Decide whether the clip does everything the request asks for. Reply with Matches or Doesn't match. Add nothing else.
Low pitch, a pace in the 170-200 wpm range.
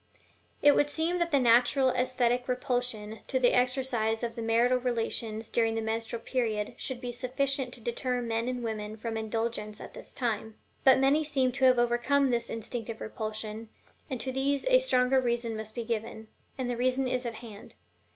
Doesn't match